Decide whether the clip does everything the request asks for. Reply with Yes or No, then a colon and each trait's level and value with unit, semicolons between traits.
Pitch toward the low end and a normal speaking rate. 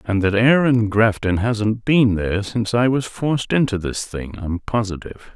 Yes: low, 110 Hz; average, 180 wpm